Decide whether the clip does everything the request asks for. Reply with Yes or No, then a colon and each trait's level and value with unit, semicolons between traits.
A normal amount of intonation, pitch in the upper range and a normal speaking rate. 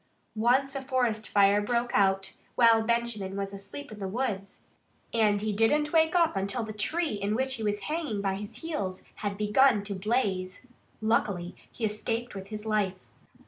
Yes: average, 3.5 semitones; high, 215 Hz; average, 175 wpm